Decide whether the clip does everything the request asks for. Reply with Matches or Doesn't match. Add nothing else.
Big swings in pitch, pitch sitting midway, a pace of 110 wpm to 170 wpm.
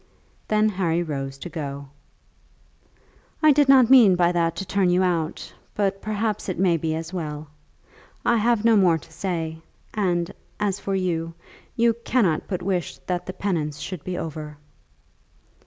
Doesn't match